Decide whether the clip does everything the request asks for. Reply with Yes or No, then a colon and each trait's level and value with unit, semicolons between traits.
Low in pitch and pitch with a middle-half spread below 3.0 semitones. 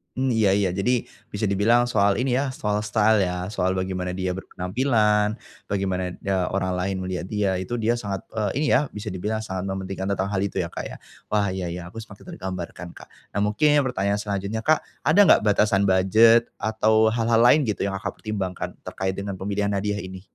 Yes: low, 100 Hz; narrow, 2.6 semitones